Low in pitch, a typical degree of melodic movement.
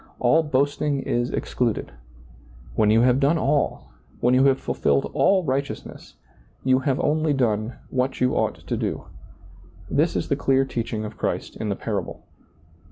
Yes: low, 130 Hz; average, 3.4 semitones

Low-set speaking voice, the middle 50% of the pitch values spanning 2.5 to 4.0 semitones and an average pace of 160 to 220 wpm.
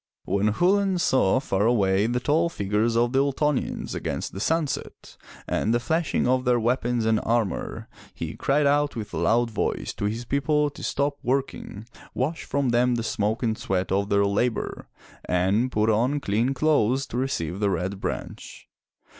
No: low, 120 Hz; average, 4.9 semitones; average, 170 wpm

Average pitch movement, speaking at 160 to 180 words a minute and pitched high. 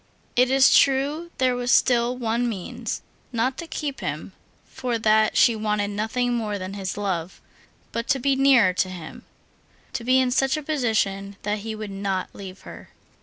Yes: average, 4.1 semitones; average, 170 wpm; high, 230 Hz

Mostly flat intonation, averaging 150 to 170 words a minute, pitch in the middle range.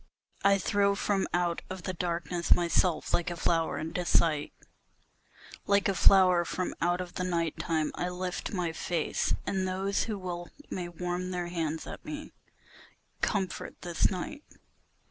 Yes: narrow, 1.7 semitones; average, 160 wpm; medium, 180 Hz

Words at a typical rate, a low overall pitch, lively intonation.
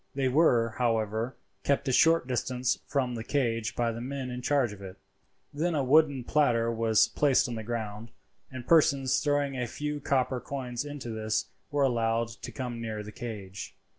No: average, 180 wpm; low, 125 Hz; average, 3.5 semitones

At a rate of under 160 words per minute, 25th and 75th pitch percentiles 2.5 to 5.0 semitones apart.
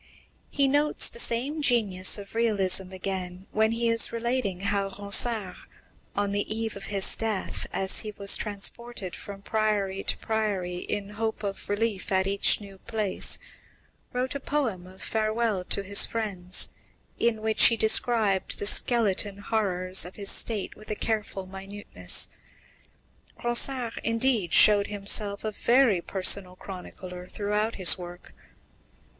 Yes: average, 140 wpm; average, 2.9 semitones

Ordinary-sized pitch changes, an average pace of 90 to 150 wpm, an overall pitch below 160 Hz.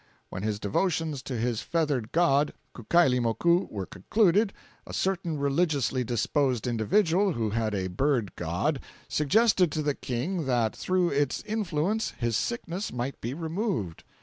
No: wide, 6.8 semitones; average, 140 wpm; medium, 140 Hz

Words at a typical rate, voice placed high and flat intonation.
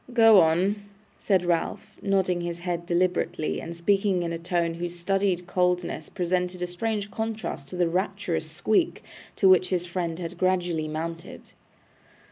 No: average, 150 wpm; medium, 180 Hz; narrow, 2.2 semitones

